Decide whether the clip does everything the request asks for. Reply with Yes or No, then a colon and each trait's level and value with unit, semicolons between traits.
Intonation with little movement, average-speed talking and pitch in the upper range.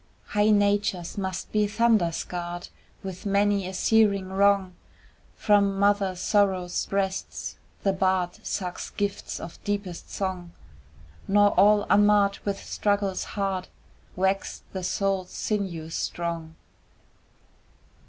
No: narrow, 1.9 semitones; slow, 110 wpm; high, 195 Hz